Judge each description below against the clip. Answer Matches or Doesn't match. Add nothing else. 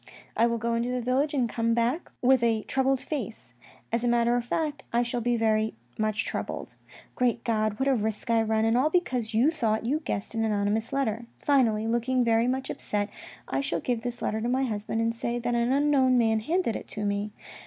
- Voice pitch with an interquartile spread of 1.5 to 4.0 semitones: Matches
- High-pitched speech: Matches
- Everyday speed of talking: Doesn't match